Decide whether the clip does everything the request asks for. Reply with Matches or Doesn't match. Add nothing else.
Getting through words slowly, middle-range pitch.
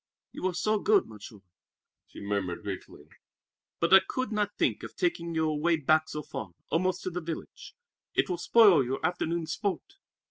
Doesn't match